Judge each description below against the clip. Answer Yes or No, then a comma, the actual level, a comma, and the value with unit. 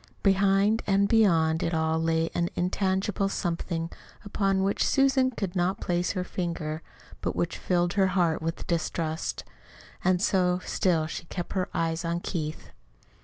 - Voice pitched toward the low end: No, medium, 180 Hz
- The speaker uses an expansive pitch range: No, average, 2.9 semitones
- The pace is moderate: Yes, average, 150 wpm